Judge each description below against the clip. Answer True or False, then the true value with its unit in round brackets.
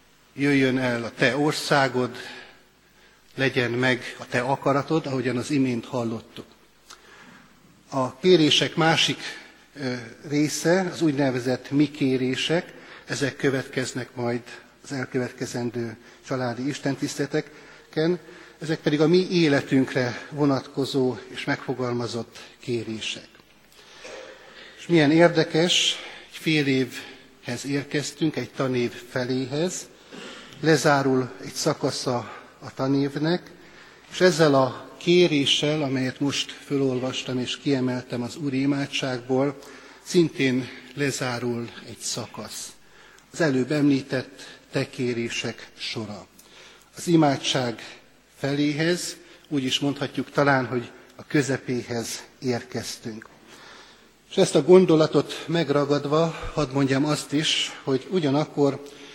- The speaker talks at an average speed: False (95 wpm)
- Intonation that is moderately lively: True (3.1 semitones)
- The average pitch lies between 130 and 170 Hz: True (140 Hz)